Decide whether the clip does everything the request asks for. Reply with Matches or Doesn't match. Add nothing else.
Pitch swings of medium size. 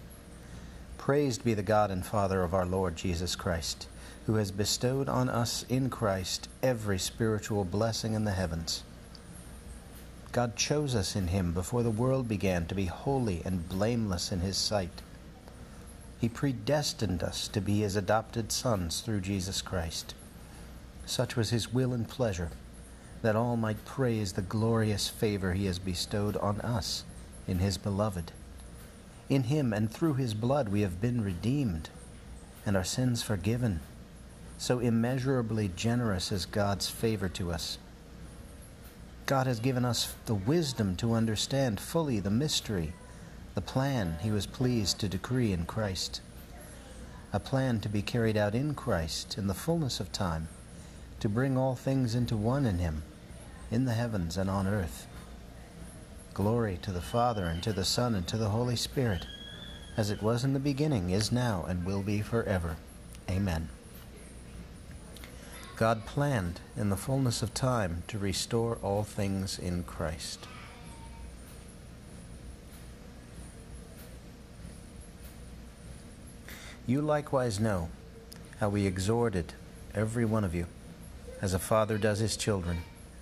Matches